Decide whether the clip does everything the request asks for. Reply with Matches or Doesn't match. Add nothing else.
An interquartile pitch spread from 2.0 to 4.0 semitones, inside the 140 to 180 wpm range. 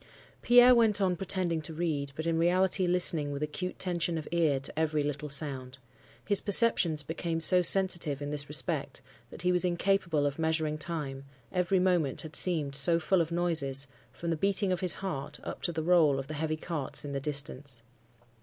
Doesn't match